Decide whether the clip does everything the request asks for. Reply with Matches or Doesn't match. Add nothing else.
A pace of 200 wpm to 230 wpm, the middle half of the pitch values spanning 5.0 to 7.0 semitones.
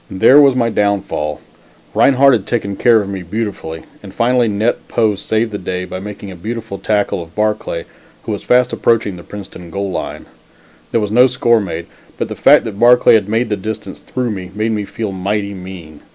Doesn't match